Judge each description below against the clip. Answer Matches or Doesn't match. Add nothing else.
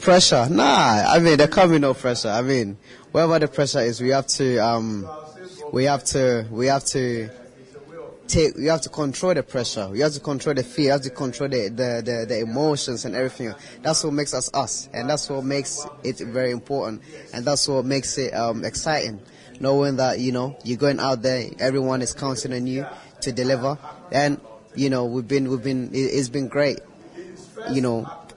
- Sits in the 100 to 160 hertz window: Matches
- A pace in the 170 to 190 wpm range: Doesn't match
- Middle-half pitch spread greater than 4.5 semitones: Doesn't match